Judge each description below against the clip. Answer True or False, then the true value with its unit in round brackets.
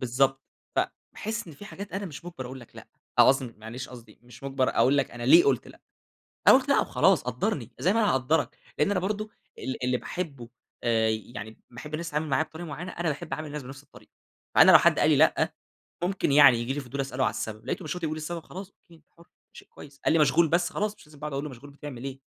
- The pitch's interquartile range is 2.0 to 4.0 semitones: False (4.6 semitones)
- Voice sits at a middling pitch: True (145 Hz)